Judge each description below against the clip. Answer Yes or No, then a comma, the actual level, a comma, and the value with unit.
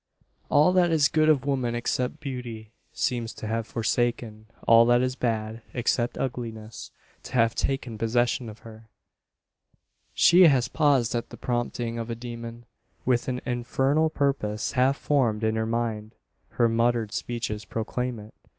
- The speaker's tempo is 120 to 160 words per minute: Yes, average, 150 wpm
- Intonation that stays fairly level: Yes, narrow, 2.2 semitones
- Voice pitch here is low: Yes, low, 120 Hz